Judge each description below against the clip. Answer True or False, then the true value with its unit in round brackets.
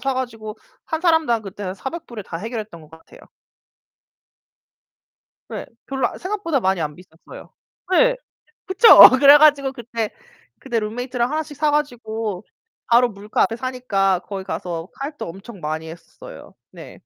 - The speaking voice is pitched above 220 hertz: True (235 Hz)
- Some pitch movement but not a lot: False (6.3 semitones)